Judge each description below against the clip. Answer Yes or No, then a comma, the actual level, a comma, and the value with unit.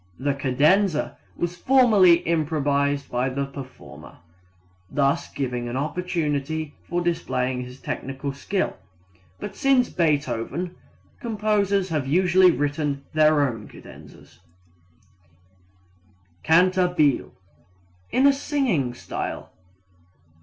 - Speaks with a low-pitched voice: No, medium, 155 Hz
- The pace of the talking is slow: Yes, slow, 95 wpm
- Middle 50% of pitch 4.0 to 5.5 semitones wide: Yes, average, 4.9 semitones